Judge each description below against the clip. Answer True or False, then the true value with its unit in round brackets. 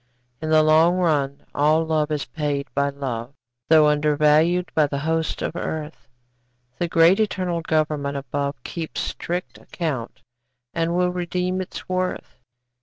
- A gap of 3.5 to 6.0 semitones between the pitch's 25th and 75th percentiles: False (3.0 semitones)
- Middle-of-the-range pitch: True (155 Hz)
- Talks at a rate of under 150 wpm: True (140 wpm)